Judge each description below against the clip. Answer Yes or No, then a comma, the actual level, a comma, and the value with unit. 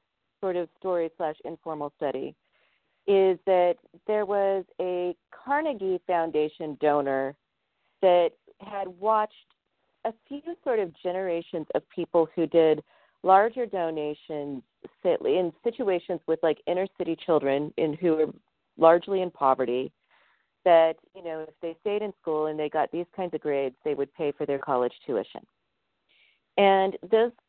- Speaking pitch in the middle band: Yes, medium, 170 Hz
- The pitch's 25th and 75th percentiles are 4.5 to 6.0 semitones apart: No, average, 3.8 semitones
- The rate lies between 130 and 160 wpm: Yes, average, 140 wpm